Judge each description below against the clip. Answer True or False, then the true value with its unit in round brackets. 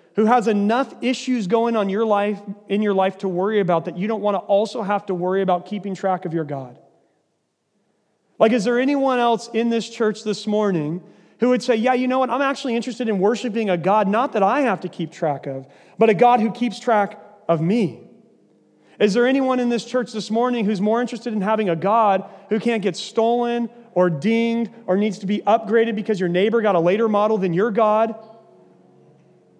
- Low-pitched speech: False (215 Hz)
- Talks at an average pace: False (215 wpm)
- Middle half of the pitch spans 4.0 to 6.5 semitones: False (2.9 semitones)